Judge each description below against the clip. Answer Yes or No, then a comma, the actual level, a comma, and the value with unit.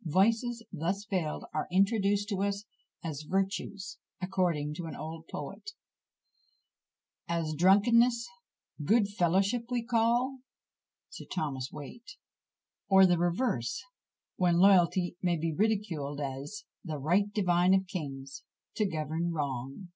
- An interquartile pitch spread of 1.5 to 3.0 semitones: No, average, 4.6 semitones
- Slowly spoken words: Yes, slow, 120 wpm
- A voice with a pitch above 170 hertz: Yes, medium, 185 Hz